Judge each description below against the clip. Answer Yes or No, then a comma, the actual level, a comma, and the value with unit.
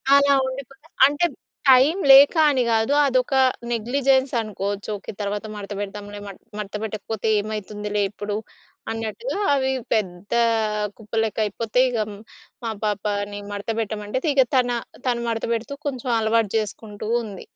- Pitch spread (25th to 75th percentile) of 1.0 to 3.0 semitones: No, average, 3.6 semitones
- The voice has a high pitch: Yes, high, 220 Hz